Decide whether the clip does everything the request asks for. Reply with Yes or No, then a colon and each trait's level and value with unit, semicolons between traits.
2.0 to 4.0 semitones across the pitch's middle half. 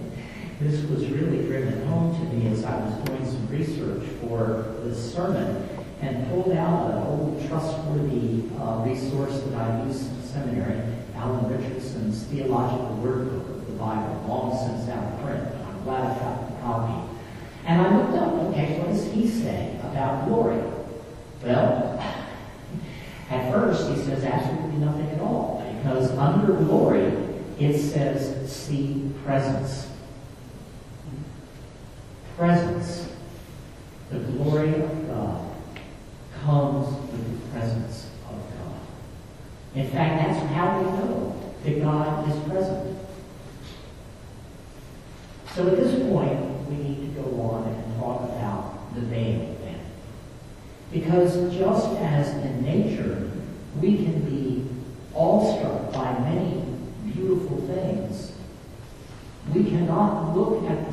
No: average, 4.8 semitones